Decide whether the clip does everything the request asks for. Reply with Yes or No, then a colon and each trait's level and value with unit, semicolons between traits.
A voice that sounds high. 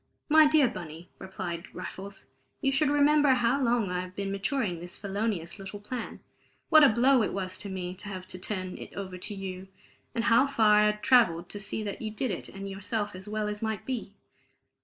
Yes: high, 205 Hz